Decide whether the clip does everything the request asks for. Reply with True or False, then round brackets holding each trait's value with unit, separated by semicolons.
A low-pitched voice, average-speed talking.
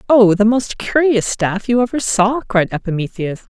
False (215 Hz; 170 wpm)